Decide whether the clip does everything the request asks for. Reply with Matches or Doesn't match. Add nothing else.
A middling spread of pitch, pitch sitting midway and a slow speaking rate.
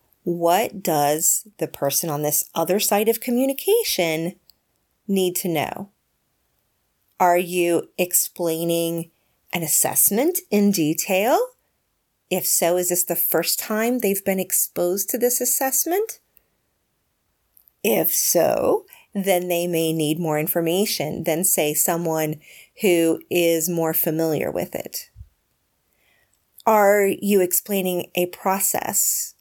Matches